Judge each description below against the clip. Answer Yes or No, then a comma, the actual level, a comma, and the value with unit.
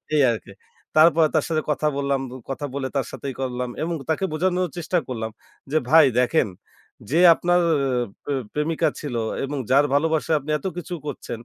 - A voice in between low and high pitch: Yes, medium, 150 Hz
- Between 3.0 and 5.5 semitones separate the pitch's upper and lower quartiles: Yes, average, 3.3 semitones